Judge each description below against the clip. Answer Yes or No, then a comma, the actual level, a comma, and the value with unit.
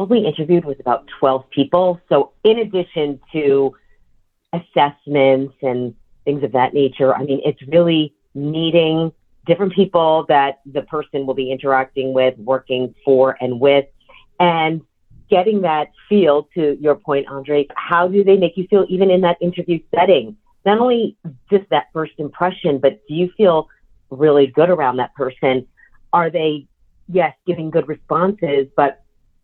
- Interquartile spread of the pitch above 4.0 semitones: Yes, average, 4.4 semitones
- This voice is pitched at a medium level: Yes, medium, 150 Hz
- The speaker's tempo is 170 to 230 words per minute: No, average, 155 wpm